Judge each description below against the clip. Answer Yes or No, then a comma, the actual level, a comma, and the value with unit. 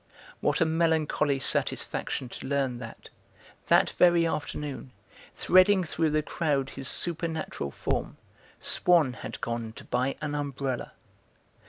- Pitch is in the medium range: Yes, medium, 145 Hz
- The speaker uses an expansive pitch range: No, average, 3.7 semitones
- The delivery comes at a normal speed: No, slow, 125 wpm